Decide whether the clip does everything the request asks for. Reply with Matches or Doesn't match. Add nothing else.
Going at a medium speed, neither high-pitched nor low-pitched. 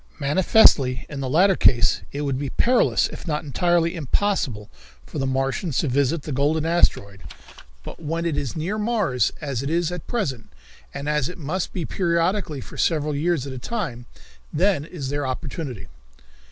Matches